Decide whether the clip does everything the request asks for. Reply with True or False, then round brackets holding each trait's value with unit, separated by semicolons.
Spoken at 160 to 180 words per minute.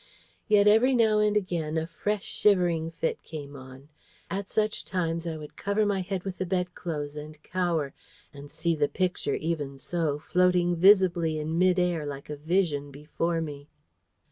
True (170 wpm)